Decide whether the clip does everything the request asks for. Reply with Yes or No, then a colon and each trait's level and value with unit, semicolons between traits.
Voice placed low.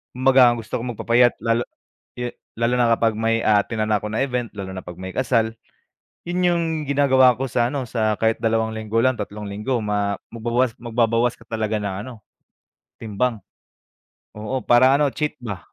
Yes: low, 115 Hz